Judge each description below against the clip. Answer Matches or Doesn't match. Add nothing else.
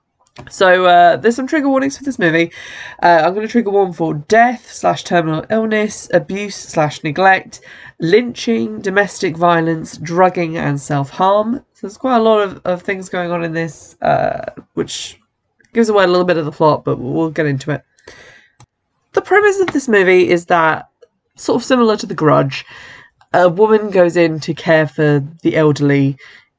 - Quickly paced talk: Doesn't match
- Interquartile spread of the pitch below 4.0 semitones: Doesn't match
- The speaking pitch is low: Doesn't match